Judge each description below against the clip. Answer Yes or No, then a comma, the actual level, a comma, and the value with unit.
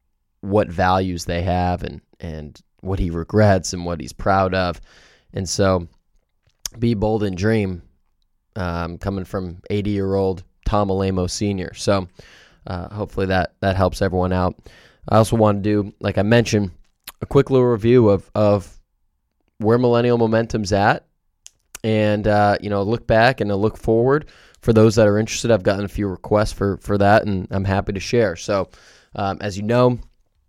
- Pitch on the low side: Yes, low, 100 Hz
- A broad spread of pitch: No, average, 2.8 semitones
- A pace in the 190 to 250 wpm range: No, average, 170 wpm